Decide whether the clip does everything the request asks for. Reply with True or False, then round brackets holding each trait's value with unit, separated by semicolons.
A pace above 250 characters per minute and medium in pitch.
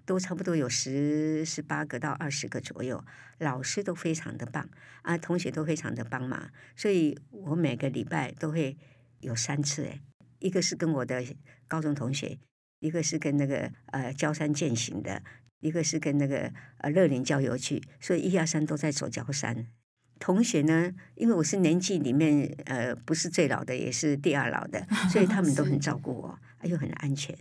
True (270 characters per minute; 150 Hz)